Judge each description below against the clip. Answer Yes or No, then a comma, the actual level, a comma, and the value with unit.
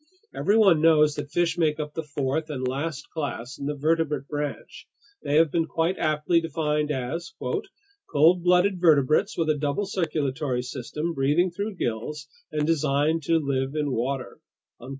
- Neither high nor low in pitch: Yes, medium, 150 Hz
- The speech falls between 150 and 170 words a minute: Yes, average, 155 wpm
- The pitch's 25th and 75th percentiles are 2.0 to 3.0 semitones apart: Yes, average, 2.7 semitones